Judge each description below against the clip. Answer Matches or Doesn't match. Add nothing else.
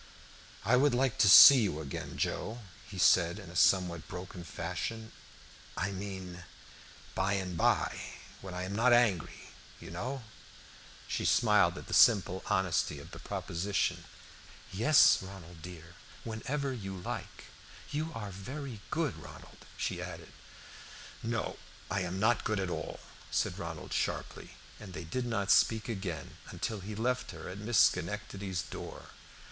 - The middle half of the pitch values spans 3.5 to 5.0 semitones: Matches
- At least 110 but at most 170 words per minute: Matches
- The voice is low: Matches